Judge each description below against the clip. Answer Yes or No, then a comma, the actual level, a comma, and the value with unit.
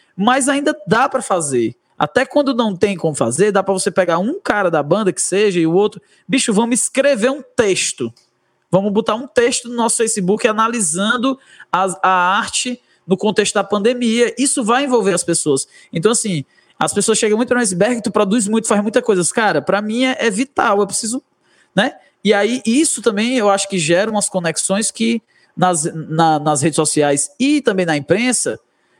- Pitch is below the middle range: No, high, 210 Hz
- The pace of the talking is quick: Yes, fast, 190 wpm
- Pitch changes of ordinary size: Yes, average, 4.5 semitones